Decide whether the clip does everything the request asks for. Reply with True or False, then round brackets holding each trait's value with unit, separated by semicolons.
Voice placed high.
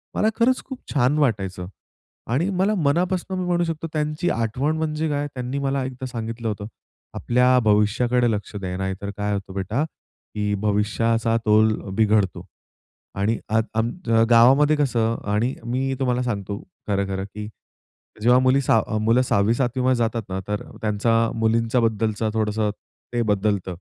False (115 Hz)